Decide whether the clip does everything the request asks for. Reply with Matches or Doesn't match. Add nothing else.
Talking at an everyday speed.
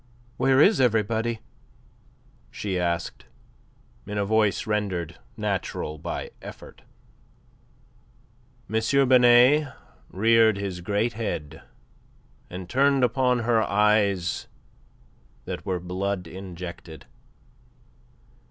Doesn't match